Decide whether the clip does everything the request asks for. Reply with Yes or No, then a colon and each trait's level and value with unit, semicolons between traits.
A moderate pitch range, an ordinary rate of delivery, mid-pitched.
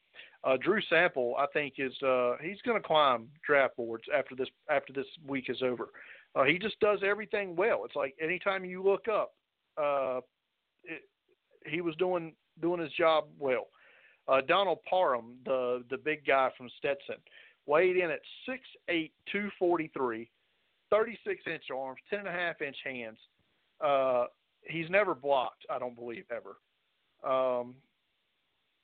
No: wide, 6.5 semitones; average, 160 wpm; medium, 155 Hz